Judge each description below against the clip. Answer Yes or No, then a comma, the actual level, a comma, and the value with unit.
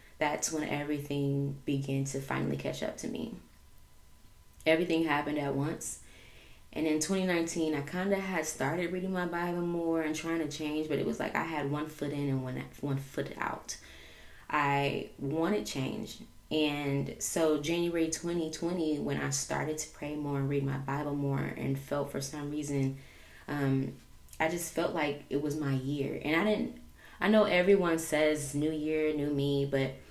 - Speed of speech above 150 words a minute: Yes, average, 175 wpm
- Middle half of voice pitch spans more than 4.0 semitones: No, average, 2.8 semitones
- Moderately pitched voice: Yes, medium, 145 Hz